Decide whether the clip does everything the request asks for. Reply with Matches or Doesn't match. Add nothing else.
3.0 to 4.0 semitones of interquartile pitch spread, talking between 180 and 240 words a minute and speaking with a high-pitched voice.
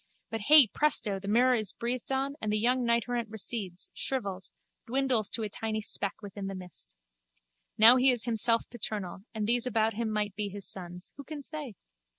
Matches